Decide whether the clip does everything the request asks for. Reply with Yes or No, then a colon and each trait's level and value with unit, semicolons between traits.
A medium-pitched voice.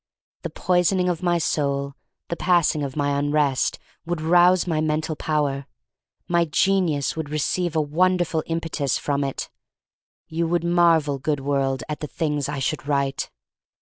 Yes: medium, 155 Hz